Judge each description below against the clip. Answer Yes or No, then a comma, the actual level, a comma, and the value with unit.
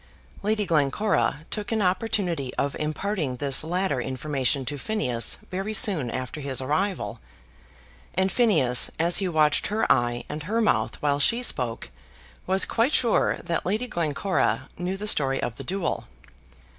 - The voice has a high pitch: No, medium, 165 Hz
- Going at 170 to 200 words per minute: No, average, 150 wpm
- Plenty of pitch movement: Yes, wide, 6.8 semitones